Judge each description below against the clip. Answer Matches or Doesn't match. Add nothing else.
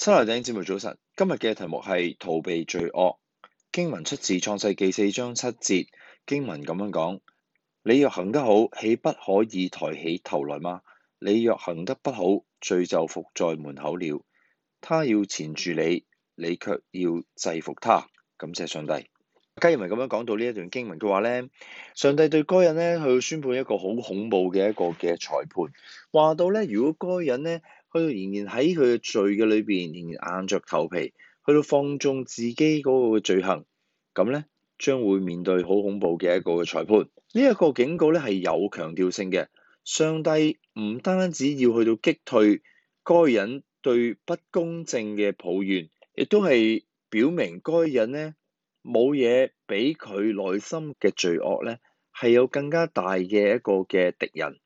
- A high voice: Doesn't match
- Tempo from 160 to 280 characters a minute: Matches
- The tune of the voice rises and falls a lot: Matches